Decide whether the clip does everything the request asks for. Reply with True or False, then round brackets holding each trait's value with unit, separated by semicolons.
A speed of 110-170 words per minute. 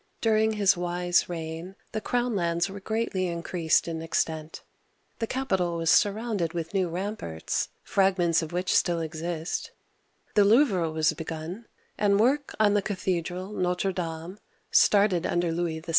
True (160 wpm)